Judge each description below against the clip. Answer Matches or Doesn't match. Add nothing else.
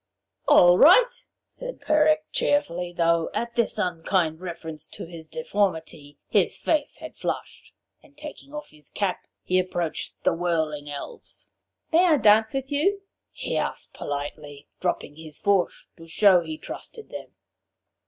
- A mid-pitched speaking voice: Matches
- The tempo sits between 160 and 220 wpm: Doesn't match